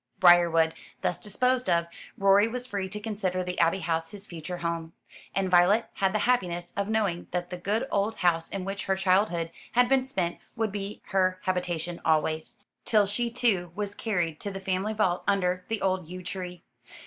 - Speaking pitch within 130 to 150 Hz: No, high, 190 Hz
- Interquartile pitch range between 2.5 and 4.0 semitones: Yes, average, 2.9 semitones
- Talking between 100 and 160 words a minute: No, average, 185 wpm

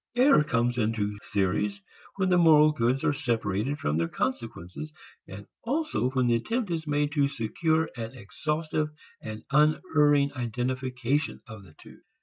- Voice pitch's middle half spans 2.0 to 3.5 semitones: No, average, 5.3 semitones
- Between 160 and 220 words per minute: No, average, 145 wpm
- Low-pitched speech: Yes, low, 130 Hz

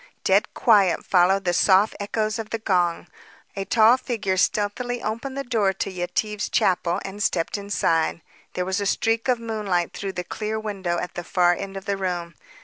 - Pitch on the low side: No, high, 200 Hz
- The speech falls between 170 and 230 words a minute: Yes, average, 185 wpm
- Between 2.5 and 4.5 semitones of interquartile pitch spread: Yes, average, 3.2 semitones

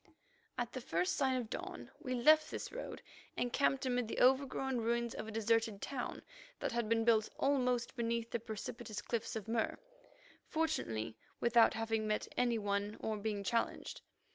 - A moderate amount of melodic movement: No, narrow, 2.3 semitones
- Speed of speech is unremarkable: Yes, average, 165 wpm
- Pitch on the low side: No, high, 230 Hz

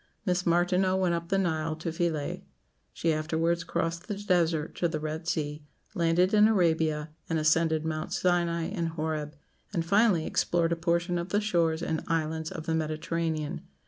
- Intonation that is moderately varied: No, narrow, 1.8 semitones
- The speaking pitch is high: No, medium, 165 Hz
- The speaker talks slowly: No, average, 170 wpm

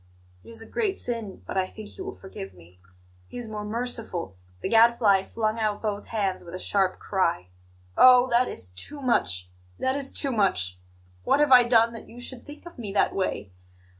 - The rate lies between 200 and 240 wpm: Yes, fast, 205 wpm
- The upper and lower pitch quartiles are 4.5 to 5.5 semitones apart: Yes, average, 4.8 semitones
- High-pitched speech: Yes, high, 215 Hz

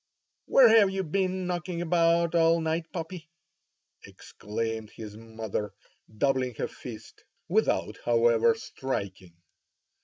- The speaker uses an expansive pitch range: Yes, wide, 7.6 semitones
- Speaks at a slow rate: Yes, slow, 110 wpm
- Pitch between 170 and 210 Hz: No, medium, 160 Hz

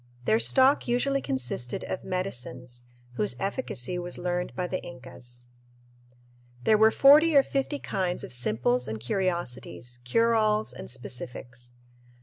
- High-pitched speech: No, medium, 175 Hz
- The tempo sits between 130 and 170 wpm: Yes, slow, 135 wpm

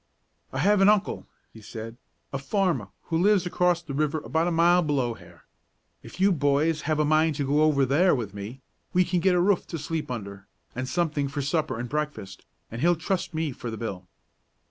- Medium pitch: Yes, medium, 150 Hz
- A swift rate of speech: Yes, fast, 210 wpm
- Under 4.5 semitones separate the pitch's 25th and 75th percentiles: No, average, 5.2 semitones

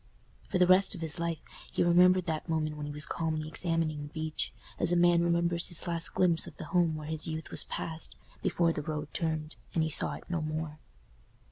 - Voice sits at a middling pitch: Yes, medium, 165 Hz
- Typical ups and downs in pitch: No, narrow, 1.8 semitones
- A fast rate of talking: Yes, fast, 220 wpm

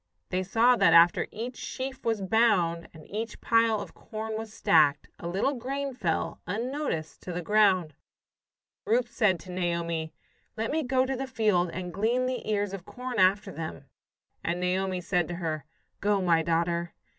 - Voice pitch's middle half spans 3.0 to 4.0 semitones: No, average, 5.1 semitones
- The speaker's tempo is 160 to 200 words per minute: Yes, average, 170 wpm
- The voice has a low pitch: No, high, 195 Hz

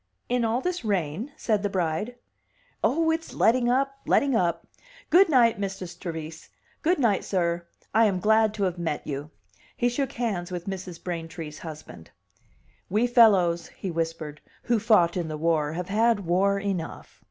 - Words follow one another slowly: No, average, 165 wpm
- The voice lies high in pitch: Yes, high, 195 Hz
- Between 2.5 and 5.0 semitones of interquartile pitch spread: No, wide, 5.6 semitones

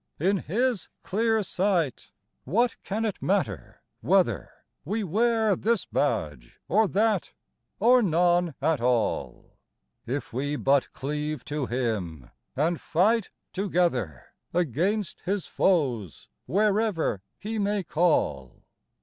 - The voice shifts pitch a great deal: Yes, wide, 7.4 semitones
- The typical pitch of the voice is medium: Yes, medium, 175 Hz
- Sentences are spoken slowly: Yes, slow, 110 wpm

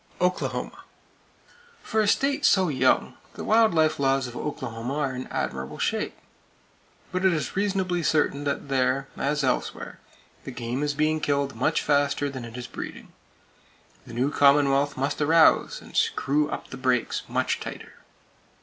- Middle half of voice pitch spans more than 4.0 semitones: No, average, 3.2 semitones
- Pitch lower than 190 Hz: Yes, medium, 140 Hz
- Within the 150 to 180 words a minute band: Yes, average, 155 wpm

